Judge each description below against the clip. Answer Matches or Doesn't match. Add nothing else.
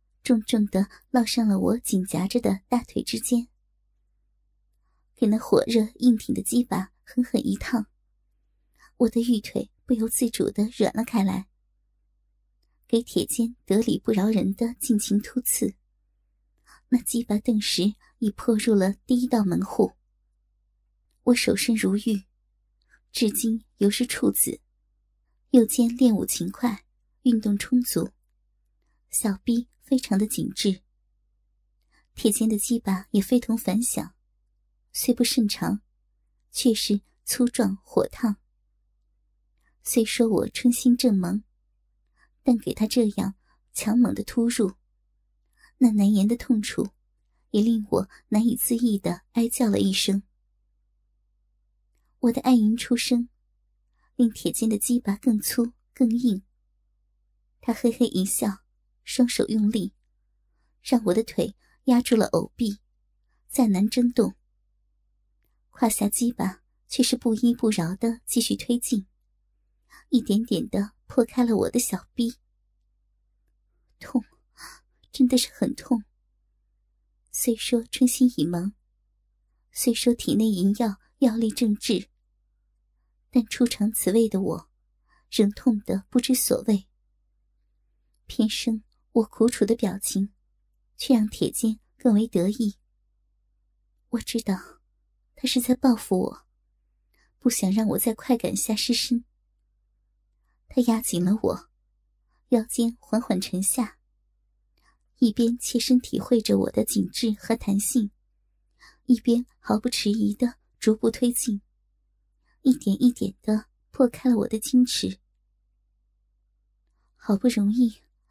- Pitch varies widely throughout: Doesn't match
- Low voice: Doesn't match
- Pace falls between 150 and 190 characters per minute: Matches